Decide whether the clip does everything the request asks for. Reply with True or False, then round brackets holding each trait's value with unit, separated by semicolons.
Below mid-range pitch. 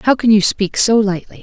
False (210 Hz)